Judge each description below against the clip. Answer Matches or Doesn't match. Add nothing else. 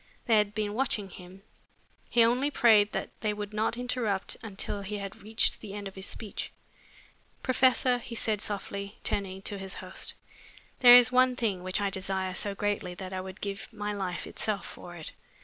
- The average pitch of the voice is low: Doesn't match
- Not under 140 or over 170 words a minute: Doesn't match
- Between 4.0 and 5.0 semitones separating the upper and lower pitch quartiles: Doesn't match